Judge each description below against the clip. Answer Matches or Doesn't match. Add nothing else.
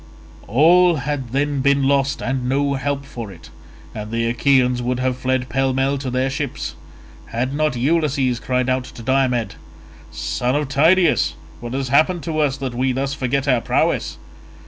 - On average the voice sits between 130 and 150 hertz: Matches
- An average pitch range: Doesn't match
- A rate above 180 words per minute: Doesn't match